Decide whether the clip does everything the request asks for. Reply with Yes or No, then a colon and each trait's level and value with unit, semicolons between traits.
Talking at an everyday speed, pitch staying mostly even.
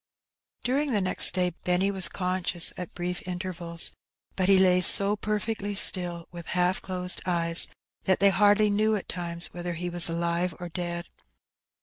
Yes: average, 170 wpm; narrow, 2.2 semitones